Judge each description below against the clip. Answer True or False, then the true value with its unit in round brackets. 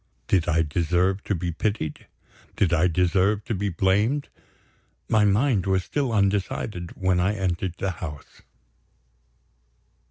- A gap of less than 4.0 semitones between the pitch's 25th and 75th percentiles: True (2.8 semitones)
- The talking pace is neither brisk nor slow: False (130 wpm)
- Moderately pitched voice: False (95 Hz)